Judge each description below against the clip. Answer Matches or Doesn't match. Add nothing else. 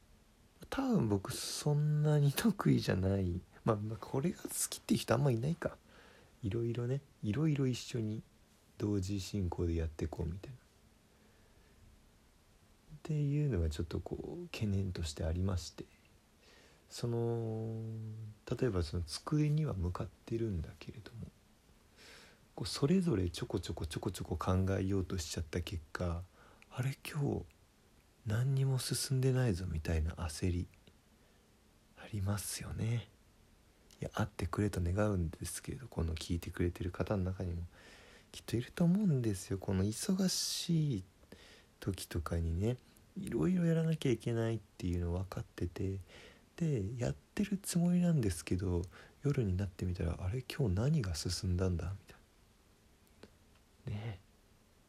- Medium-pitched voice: Doesn't match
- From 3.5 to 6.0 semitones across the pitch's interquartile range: Matches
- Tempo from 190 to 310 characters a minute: Matches